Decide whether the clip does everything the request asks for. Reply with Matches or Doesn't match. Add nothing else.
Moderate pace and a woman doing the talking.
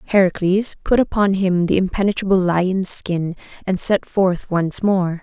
Matches